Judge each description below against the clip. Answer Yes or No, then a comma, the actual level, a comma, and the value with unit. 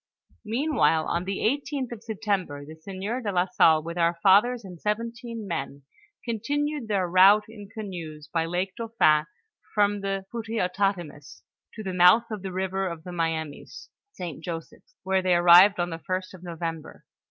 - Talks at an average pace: Yes, average, 165 wpm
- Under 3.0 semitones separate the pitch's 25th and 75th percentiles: No, average, 4.3 semitones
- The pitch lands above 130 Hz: Yes, high, 190 Hz